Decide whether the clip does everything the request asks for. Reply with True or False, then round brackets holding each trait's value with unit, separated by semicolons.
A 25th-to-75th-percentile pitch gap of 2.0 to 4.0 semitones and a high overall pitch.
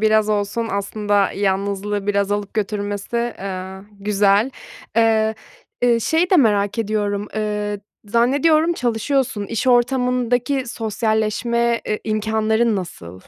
True (2.7 semitones; 215 Hz)